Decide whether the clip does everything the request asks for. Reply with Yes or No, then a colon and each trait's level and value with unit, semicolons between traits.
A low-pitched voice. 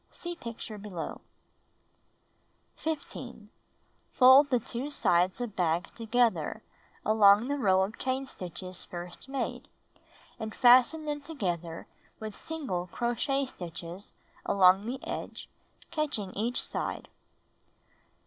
No: high, 225 Hz